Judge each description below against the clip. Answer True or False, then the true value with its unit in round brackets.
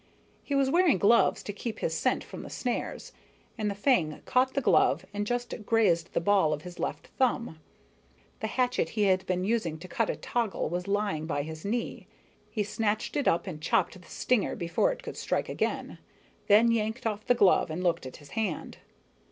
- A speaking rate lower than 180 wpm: False (200 wpm)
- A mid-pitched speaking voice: False (205 Hz)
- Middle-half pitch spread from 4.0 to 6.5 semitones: True (5.2 semitones)